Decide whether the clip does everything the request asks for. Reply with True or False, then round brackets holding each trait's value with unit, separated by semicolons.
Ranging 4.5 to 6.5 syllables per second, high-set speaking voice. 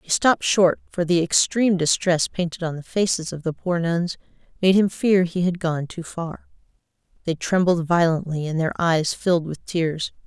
False (4.8 syllables/s; 170 Hz)